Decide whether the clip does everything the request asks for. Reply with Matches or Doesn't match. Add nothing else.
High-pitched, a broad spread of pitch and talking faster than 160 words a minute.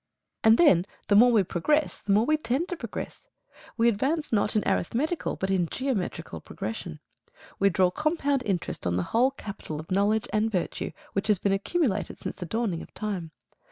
Matches